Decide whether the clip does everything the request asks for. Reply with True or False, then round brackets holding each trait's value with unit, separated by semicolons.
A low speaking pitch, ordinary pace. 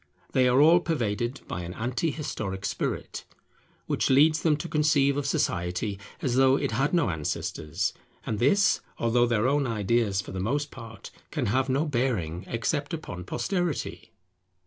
True (125 Hz; 160 wpm)